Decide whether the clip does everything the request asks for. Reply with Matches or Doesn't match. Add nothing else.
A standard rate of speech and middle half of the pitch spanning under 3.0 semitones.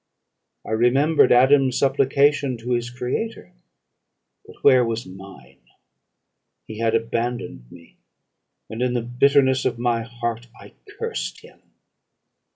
Doesn't match